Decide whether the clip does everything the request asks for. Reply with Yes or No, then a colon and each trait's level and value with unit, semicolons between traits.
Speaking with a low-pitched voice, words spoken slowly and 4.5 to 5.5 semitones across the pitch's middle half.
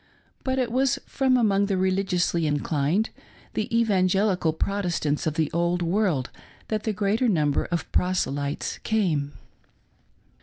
No: medium, 185 Hz; slow, 130 wpm; average, 5.1 semitones